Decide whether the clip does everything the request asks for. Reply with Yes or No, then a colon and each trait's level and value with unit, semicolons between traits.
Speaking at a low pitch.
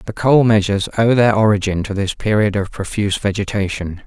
Yes: low, 105 Hz